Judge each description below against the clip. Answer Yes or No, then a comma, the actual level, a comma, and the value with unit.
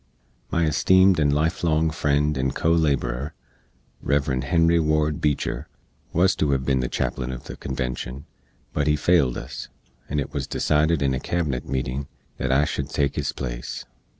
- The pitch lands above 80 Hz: No, very low, 75 Hz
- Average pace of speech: Yes, average, 170 wpm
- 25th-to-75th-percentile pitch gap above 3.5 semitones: No, average, 2.9 semitones